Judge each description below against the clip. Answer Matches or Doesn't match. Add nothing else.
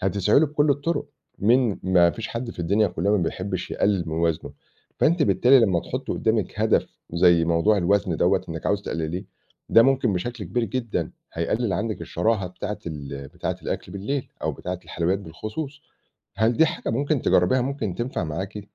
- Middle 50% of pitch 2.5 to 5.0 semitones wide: Doesn't match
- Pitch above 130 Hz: Doesn't match